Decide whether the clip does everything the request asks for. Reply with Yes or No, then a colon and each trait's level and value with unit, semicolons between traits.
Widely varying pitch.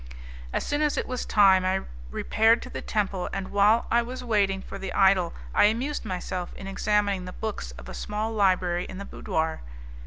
No: average, 2.9 semitones